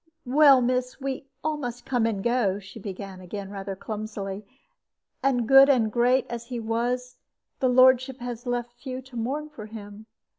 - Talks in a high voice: Yes, high, 240 Hz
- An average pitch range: Yes, average, 3.2 semitones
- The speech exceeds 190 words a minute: No, average, 170 wpm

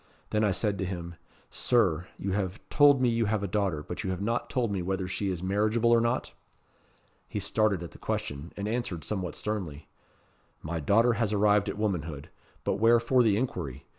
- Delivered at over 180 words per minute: Yes, average, 195 wpm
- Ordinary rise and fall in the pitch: Yes, average, 4.0 semitones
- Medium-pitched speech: No, low, 100 Hz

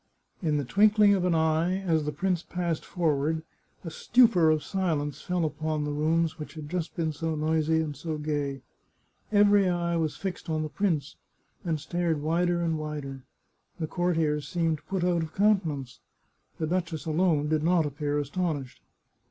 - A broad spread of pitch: No, average, 2.7 semitones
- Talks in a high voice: No, medium, 160 Hz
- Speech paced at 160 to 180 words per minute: Yes, average, 170 wpm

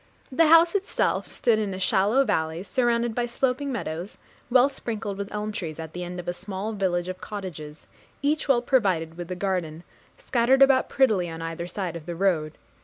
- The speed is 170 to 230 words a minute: Yes, average, 190 wpm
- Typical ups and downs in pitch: No, wide, 5.7 semitones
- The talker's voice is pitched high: Yes, high, 195 Hz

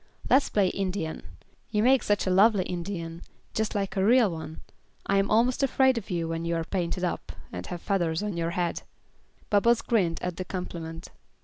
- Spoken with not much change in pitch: No, average, 3.8 semitones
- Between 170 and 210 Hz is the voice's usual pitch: Yes, medium, 185 Hz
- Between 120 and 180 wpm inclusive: No, average, 190 wpm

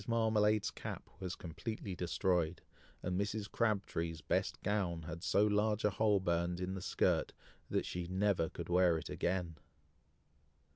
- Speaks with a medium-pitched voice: No, very low, 95 Hz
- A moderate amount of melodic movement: Yes, average, 3.3 semitones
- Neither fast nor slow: Yes, average, 145 wpm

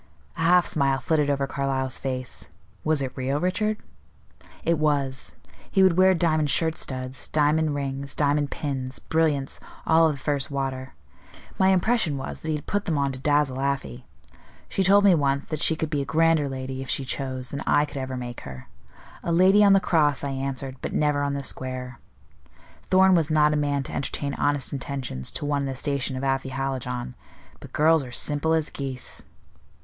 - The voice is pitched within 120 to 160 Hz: Yes, medium, 140 Hz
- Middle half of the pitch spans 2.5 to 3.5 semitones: Yes, average, 3.0 semitones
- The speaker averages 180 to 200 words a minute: Yes, average, 190 wpm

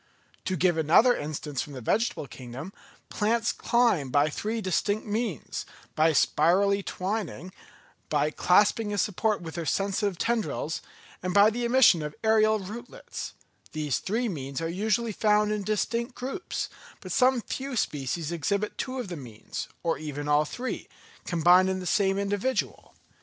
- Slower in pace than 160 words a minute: Yes, average, 150 wpm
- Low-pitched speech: No, high, 195 Hz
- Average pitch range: No, wide, 5.8 semitones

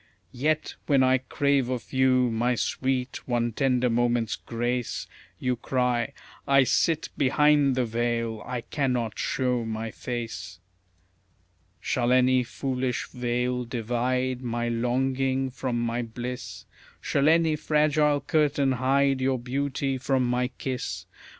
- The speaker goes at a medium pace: No, slow, 125 wpm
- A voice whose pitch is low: Yes, low, 125 Hz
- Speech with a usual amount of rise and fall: No, narrow, 1.9 semitones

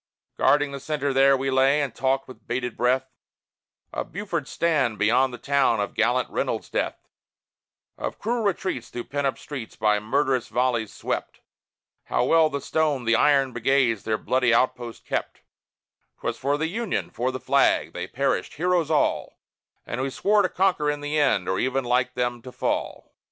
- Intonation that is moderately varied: Yes, average, 3.2 semitones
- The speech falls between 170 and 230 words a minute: Yes, average, 175 wpm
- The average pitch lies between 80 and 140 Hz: Yes, low, 135 Hz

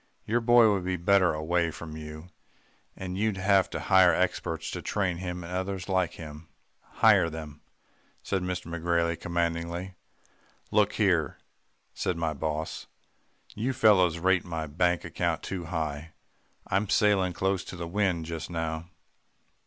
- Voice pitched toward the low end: Yes, very low, 90 Hz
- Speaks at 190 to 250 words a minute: No, average, 145 wpm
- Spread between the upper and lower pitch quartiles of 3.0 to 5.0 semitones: No, narrow, 2.6 semitones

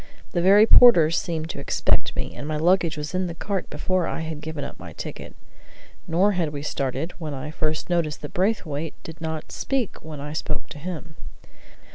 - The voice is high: No, medium, 160 Hz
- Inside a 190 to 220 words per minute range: Yes, average, 195 wpm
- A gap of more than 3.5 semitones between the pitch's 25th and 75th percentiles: No, average, 3.0 semitones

